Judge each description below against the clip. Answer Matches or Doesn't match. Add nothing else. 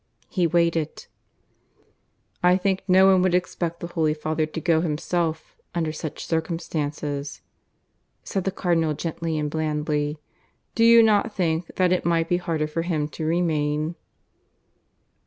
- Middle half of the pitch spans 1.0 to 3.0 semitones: Matches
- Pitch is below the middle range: Doesn't match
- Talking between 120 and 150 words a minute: Matches